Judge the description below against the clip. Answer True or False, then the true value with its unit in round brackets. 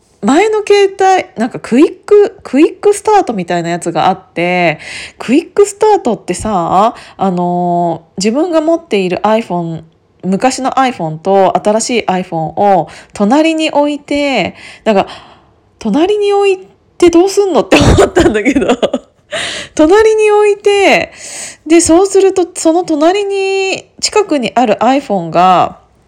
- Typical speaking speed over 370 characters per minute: False (300 characters per minute)